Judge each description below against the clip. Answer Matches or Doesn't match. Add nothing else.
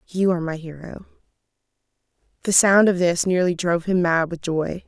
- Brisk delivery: Doesn't match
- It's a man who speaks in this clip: Doesn't match